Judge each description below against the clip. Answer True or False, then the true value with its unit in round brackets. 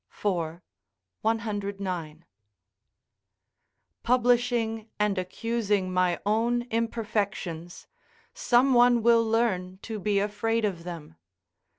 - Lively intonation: False (3.9 semitones)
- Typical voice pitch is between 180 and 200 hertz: False (210 Hz)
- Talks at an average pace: False (85 wpm)